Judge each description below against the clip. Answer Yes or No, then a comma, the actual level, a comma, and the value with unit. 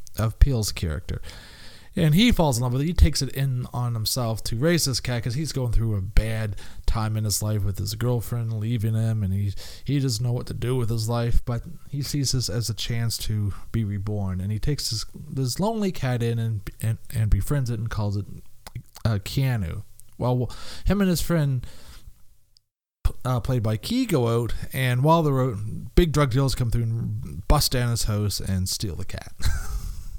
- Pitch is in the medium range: No, low, 115 Hz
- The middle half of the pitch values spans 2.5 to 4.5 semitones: Yes, average, 3.8 semitones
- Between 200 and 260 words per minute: Yes, fast, 205 wpm